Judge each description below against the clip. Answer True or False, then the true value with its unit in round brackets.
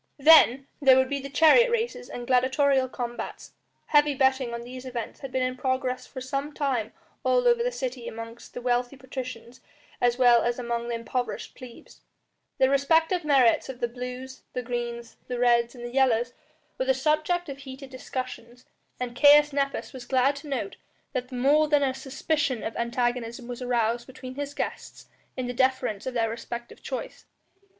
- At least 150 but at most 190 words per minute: True (175 wpm)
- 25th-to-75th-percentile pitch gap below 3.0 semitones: True (2.4 semitones)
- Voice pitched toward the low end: False (255 Hz)